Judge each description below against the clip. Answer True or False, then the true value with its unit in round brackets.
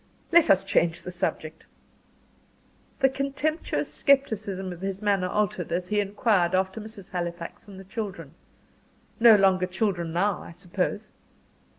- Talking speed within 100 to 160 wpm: True (135 wpm)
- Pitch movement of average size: True (3.0 semitones)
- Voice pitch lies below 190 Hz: False (195 Hz)